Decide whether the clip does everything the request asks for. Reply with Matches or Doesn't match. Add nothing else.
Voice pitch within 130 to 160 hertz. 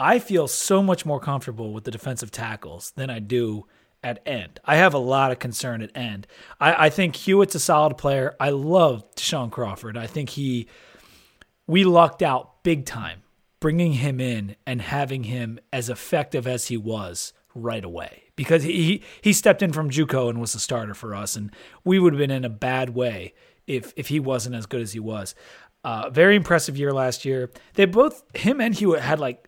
Matches